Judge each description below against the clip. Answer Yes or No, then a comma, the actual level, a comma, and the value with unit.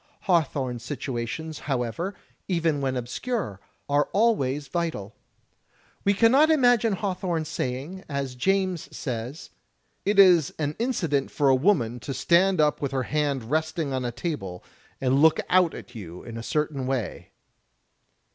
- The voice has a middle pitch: Yes, medium, 150 Hz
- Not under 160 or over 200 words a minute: No, average, 145 wpm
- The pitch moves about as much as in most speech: No, wide, 6.0 semitones